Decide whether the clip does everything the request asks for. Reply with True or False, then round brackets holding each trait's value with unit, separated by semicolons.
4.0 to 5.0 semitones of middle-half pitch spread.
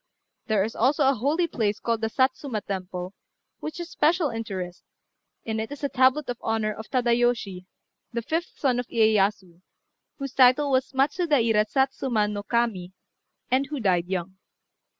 True (4.6 semitones)